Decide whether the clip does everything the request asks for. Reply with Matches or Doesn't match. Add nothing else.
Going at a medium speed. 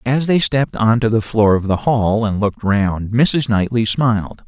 Doesn't match